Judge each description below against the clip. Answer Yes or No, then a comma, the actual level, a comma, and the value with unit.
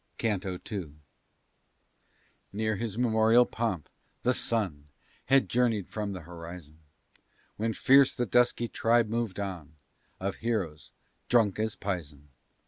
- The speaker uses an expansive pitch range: No, average, 4.5 semitones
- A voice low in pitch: Yes, low, 105 Hz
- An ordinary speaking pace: No, slow, 120 wpm